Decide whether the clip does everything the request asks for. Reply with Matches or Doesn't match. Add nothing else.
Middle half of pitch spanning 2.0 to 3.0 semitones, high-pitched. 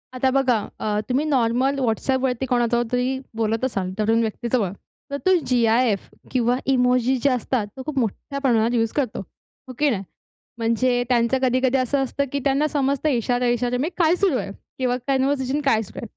Matches